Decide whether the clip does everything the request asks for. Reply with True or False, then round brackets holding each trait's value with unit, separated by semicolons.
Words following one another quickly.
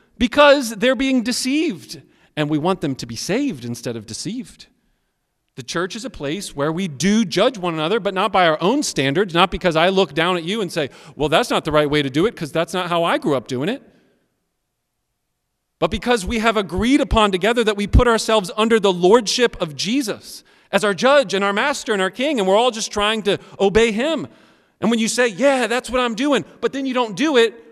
True (230 wpm)